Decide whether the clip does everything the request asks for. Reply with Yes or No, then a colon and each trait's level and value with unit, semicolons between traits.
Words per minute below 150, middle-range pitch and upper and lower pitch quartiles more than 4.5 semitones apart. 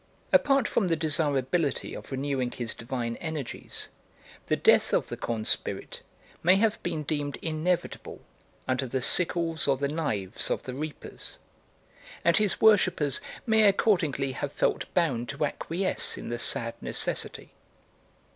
Yes: average, 140 wpm; medium, 150 Hz; average, 4.9 semitones